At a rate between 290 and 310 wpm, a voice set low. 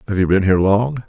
No: fast, 280 wpm; low, 105 Hz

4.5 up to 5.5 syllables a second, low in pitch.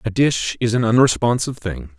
Yes: 5.4 syllables/s; low, 110 Hz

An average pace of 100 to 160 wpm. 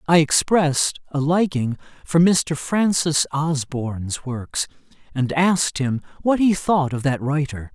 Yes: average, 140 wpm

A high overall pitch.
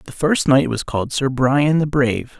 No: low, 135 Hz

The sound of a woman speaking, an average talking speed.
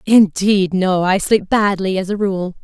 Yes: female; average, 180 wpm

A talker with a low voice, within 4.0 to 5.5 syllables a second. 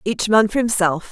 No: high, 205 Hz; 5.0 syllables/s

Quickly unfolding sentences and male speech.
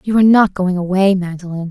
No: fast, 210 wpm; female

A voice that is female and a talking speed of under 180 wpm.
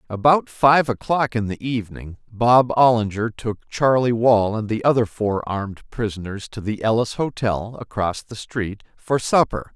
No: male; average, 160 wpm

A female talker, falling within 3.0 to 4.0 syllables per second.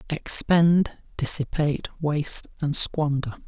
No: male; 3.9 syllables/s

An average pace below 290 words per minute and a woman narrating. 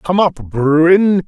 No: average, 140 wpm; male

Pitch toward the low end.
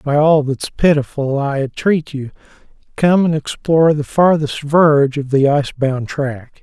No: medium, 145 Hz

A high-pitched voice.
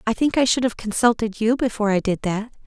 Yes: high, 225 Hz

